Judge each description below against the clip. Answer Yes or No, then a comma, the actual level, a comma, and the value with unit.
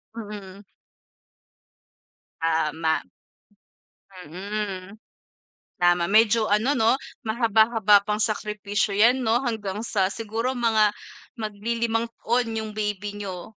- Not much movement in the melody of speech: Yes, narrow, 2.2 semitones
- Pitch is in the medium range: No, high, 210 Hz